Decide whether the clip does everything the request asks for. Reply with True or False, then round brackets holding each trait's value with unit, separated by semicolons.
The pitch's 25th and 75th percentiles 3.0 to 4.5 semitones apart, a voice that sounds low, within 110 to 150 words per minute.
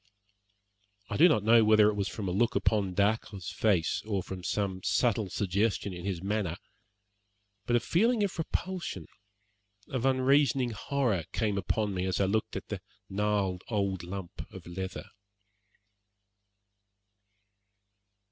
True (3.8 semitones; 105 Hz; 140 wpm)